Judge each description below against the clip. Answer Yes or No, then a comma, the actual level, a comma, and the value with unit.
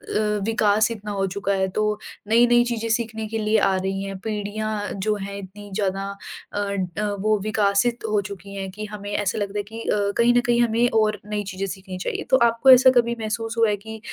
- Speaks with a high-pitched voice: Yes, high, 210 Hz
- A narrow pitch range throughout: Yes, narrow, 2.2 semitones